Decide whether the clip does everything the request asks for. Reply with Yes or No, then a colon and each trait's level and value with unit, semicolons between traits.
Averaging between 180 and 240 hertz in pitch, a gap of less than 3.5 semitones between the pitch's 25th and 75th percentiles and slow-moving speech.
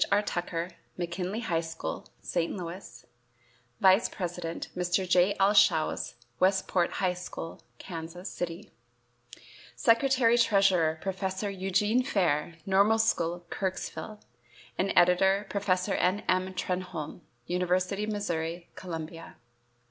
Yes: medium, 185 Hz; narrow, 2.4 semitones; slow, 110 wpm